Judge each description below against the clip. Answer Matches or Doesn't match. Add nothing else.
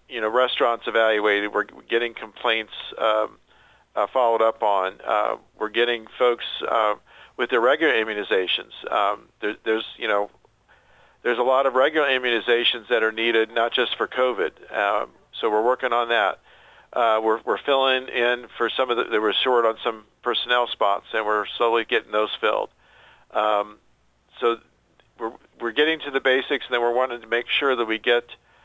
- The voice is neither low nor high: Doesn't match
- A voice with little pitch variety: Matches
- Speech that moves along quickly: Doesn't match